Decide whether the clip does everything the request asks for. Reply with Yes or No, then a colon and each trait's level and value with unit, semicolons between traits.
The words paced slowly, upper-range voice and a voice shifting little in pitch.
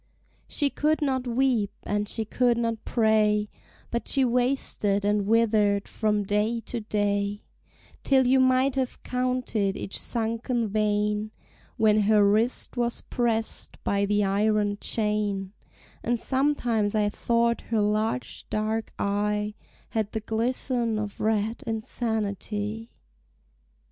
Yes: slow, 125 wpm; high, 220 Hz; narrow, 2.3 semitones